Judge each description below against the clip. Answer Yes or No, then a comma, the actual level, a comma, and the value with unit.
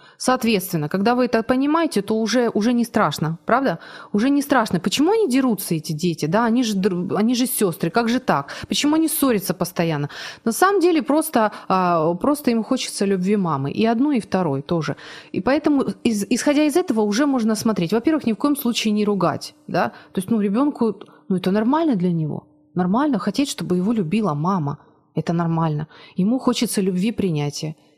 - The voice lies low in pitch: No, high, 215 Hz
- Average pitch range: No, wide, 5.9 semitones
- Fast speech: Yes, fast, 180 wpm